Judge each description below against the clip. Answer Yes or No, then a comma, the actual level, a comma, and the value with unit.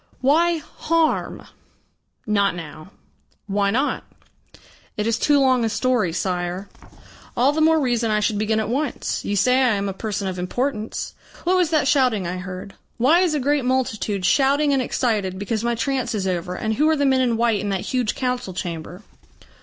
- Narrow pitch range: No, average, 5.3 semitones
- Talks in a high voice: Yes, high, 230 Hz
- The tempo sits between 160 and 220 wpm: Yes, average, 185 wpm